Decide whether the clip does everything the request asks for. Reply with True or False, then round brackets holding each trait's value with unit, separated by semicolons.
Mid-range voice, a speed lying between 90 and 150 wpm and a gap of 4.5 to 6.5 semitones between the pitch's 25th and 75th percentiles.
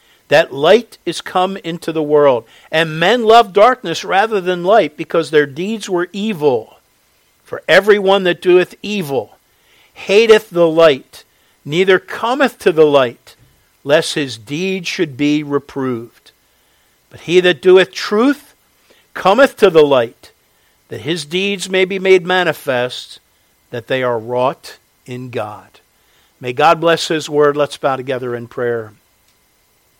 True (170 Hz; 140 wpm; 5.3 semitones)